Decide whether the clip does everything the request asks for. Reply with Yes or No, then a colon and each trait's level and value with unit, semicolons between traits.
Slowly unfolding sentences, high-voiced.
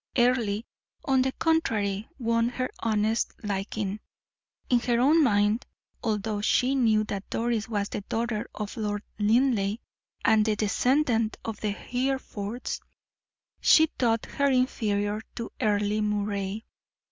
Yes: slow, 125 wpm; high, 220 Hz